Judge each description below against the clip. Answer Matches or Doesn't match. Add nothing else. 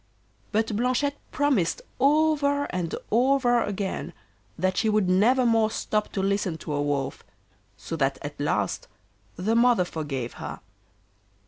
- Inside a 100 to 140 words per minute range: Matches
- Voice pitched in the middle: Doesn't match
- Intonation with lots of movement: Matches